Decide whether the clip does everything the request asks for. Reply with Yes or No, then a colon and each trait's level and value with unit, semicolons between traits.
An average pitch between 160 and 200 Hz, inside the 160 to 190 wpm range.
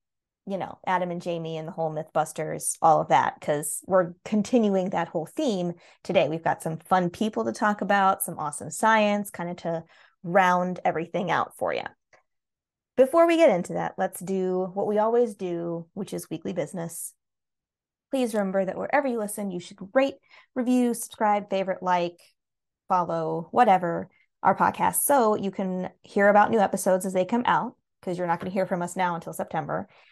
Yes: high, 190 Hz; average, 185 wpm